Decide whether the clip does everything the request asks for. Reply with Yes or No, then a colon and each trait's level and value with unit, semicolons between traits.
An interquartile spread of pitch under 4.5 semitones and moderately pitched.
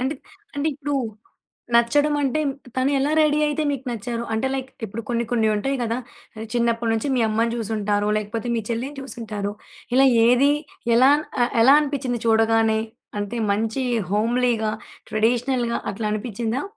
No: average, 3.2 semitones; high, 235 Hz